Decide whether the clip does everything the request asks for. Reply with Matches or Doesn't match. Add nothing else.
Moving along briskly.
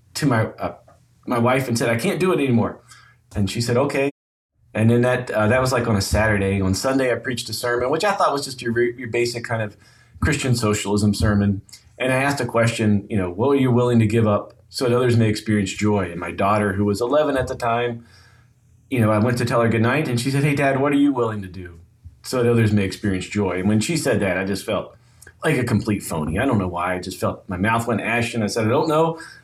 Matches